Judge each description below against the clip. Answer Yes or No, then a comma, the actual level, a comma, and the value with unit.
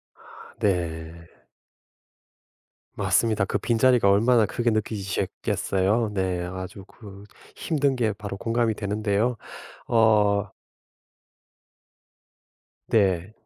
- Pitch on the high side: No, low, 105 Hz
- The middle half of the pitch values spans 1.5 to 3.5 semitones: Yes, average, 2.9 semitones